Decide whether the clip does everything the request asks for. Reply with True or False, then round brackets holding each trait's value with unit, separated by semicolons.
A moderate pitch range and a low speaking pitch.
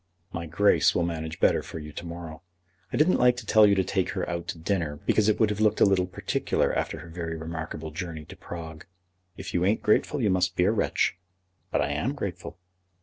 True (4.0 semitones; 90 Hz)